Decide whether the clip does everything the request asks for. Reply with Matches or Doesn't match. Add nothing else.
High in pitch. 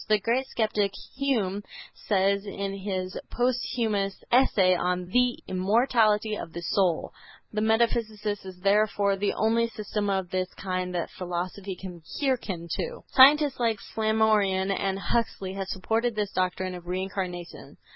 Matches